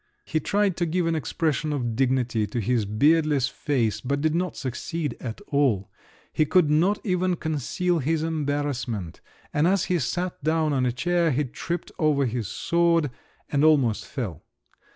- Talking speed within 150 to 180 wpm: Yes, average, 165 wpm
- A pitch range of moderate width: Yes, average, 4.7 semitones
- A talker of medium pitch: Yes, medium, 150 Hz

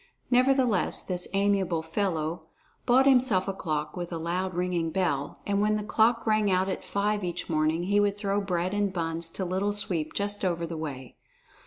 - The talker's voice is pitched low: No, medium, 185 Hz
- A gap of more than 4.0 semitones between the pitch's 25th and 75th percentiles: No, average, 3.6 semitones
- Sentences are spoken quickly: No, average, 185 wpm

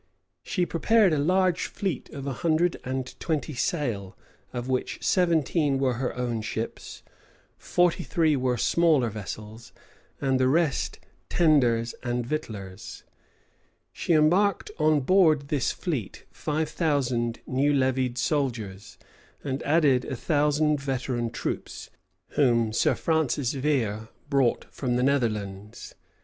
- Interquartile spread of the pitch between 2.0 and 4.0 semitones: No, average, 4.5 semitones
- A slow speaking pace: Yes, slow, 125 wpm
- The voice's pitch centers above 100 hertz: Yes, low, 135 Hz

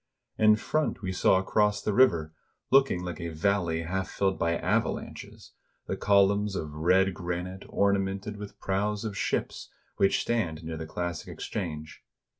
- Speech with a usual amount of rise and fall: Yes, average, 3.4 semitones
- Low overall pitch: Yes, very low, 95 Hz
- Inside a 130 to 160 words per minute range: Yes, average, 150 wpm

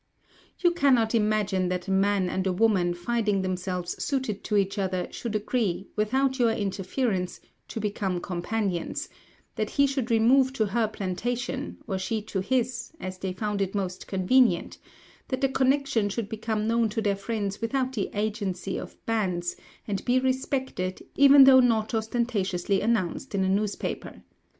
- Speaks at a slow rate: No, average, 160 wpm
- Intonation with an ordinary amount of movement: Yes, average, 4.1 semitones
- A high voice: Yes, high, 215 Hz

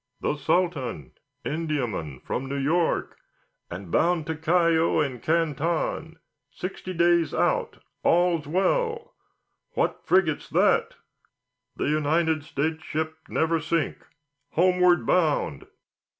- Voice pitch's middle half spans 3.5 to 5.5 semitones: No, average, 2.9 semitones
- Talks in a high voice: No, medium, 160 Hz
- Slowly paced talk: Yes, slow, 100 wpm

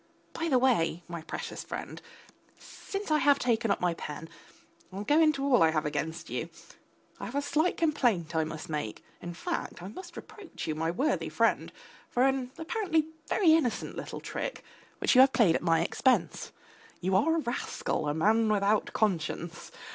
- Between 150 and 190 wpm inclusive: Yes, average, 180 wpm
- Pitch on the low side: No, high, 225 Hz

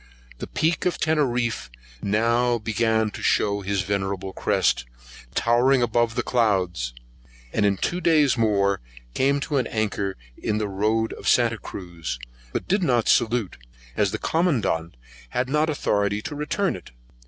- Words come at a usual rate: Yes, average, 150 wpm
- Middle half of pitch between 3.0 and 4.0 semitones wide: No, average, 4.4 semitones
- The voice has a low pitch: Yes, low, 115 Hz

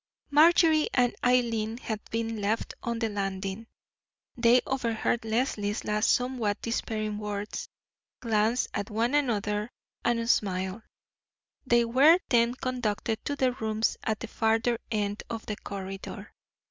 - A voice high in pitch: Yes, high, 225 Hz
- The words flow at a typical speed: No, slow, 130 wpm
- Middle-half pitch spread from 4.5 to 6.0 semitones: No, narrow, 2.6 semitones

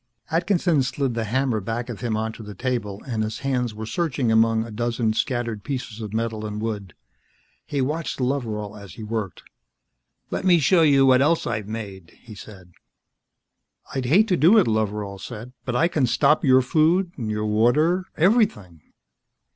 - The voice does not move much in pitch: No, average, 4.5 semitones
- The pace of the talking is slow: No, average, 170 wpm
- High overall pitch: No, low, 120 Hz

